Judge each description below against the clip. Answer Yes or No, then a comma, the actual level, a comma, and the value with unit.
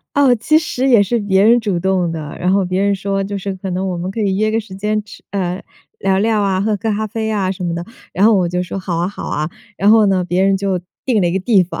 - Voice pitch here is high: Yes, high, 195 Hz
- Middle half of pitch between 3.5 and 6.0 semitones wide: No, narrow, 2.6 semitones